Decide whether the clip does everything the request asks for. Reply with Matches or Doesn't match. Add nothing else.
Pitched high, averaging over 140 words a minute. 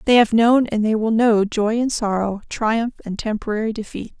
Matches